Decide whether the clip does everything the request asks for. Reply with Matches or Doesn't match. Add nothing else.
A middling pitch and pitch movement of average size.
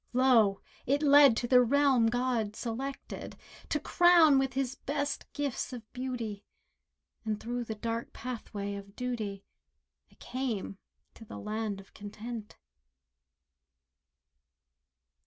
Doesn't match